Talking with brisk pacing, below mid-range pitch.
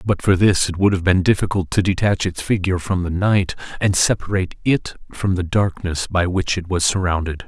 Yes: fast, 210 wpm; very low, 90 Hz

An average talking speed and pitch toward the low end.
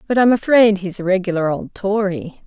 No: average, 195 wpm; high, 200 Hz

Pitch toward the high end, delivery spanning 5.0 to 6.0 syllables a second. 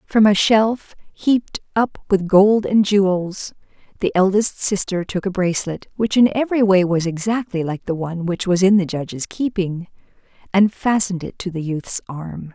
No: high, 195 Hz; 4.8 syllables/s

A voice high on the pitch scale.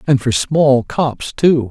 No: low, 135 Hz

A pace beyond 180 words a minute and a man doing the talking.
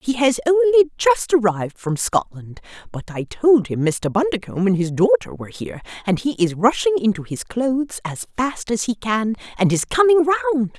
No: average, 190 wpm; female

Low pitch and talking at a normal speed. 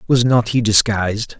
Yes: low, 110 Hz; average, 170 wpm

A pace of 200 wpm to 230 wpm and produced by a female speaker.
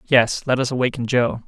No: fast, 205 wpm; male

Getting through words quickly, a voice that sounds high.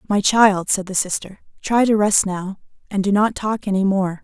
Yes: fast, 210 wpm; high, 200 Hz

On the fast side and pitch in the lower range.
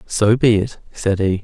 Yes: fast, 210 wpm; low, 105 Hz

